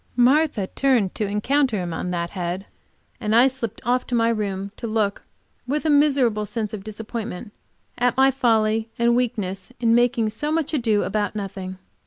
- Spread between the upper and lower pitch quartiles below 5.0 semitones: Yes, average, 3.4 semitones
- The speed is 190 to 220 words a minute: No, average, 175 wpm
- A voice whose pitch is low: No, high, 225 Hz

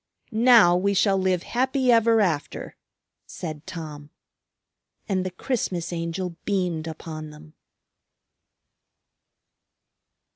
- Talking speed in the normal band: No, slow, 95 wpm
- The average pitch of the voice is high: No, medium, 180 Hz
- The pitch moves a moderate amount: Yes, average, 4.3 semitones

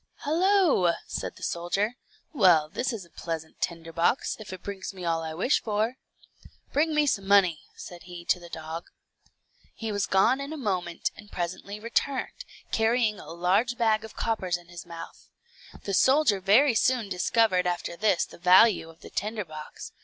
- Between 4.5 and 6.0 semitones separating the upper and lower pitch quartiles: Yes, average, 4.9 semitones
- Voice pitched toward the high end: Yes, high, 195 Hz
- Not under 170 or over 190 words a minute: Yes, average, 175 wpm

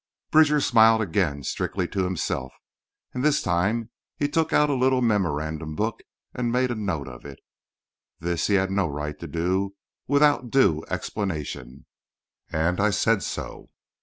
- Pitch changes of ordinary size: No, wide, 7.4 semitones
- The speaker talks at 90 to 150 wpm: Yes, average, 145 wpm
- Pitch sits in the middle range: No, low, 100 Hz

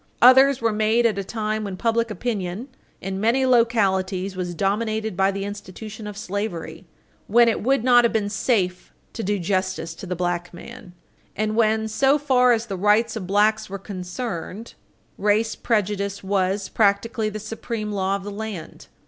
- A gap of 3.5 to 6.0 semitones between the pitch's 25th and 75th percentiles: No, average, 3.0 semitones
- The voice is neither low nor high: No, high, 210 Hz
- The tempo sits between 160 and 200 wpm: Yes, average, 170 wpm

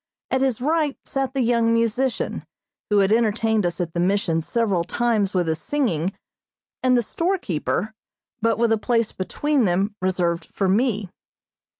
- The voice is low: No, high, 220 Hz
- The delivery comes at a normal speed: Yes, average, 160 wpm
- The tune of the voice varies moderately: Yes, average, 4.6 semitones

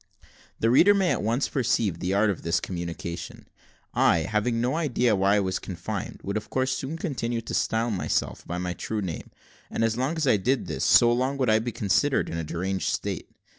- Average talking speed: No, fast, 210 wpm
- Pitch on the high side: No, low, 110 Hz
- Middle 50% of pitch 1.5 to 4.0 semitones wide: No, average, 5.3 semitones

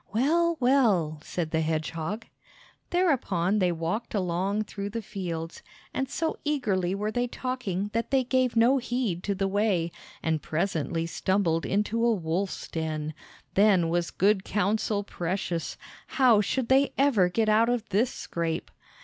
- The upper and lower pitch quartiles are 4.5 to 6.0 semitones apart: Yes, wide, 5.6 semitones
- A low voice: No, high, 200 Hz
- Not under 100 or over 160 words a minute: Yes, average, 150 wpm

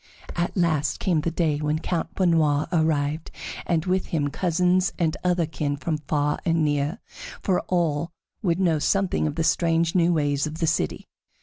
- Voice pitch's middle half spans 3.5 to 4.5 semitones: No, narrow, 2.6 semitones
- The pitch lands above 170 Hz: No, medium, 165 Hz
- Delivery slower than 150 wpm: No, average, 175 wpm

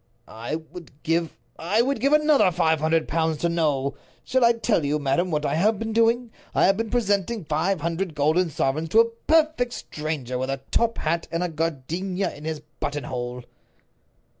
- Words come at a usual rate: Yes, average, 180 wpm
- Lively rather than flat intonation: Yes, wide, 6.5 semitones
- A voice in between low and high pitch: Yes, medium, 165 Hz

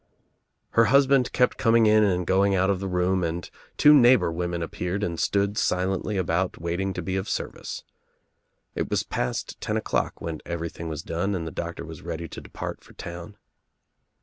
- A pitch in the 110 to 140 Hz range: No, very low, 90 Hz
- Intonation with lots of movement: No, average, 3.1 semitones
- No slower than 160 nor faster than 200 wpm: Yes, average, 185 wpm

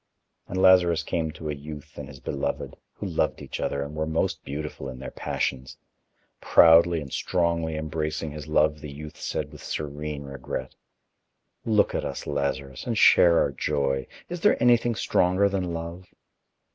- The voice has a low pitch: Yes, very low, 75 Hz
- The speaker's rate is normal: Yes, average, 165 wpm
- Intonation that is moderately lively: Yes, average, 3.1 semitones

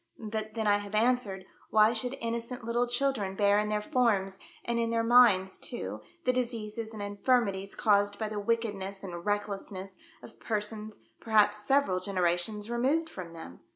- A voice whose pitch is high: Yes, high, 215 Hz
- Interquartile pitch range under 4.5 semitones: Yes, narrow, 2.6 semitones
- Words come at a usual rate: Yes, average, 165 wpm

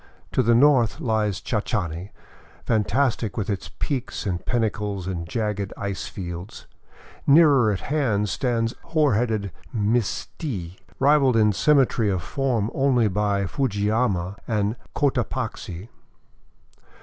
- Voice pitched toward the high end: No, low, 110 Hz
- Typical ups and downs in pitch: Yes, average, 4.1 semitones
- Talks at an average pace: No, slow, 115 wpm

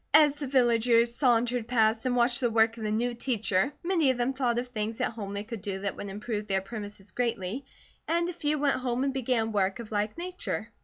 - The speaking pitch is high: Yes, high, 235 Hz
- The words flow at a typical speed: No, fast, 225 wpm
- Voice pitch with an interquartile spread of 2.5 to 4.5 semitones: Yes, average, 3.4 semitones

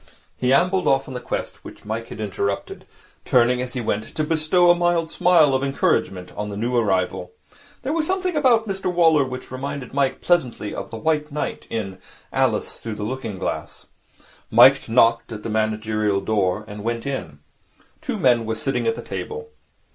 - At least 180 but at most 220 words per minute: Yes, average, 185 wpm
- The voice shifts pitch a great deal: Yes, wide, 6.9 semitones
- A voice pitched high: No, low, 125 Hz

